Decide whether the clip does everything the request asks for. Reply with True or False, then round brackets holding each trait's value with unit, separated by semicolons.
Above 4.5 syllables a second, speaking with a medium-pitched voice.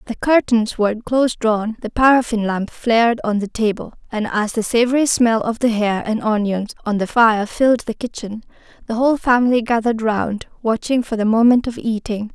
False (5.3 syllables/s; 225 Hz)